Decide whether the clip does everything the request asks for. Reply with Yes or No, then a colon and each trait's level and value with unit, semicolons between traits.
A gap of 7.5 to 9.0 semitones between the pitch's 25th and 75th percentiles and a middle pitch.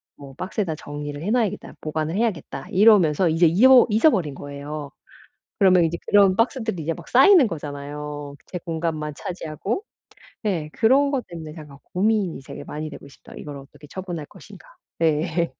No: wide, 5.6 semitones; medium, 165 Hz